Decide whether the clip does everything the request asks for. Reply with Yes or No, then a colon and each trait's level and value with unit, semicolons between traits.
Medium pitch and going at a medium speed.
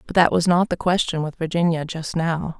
No: medium, 170 Hz; fast, 230 wpm